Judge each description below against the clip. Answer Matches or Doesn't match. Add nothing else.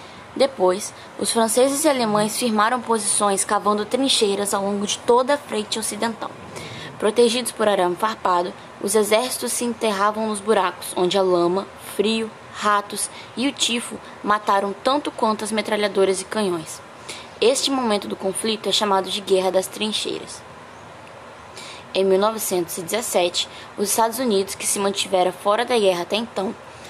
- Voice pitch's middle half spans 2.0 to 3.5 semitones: Matches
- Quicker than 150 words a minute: Doesn't match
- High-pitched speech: Matches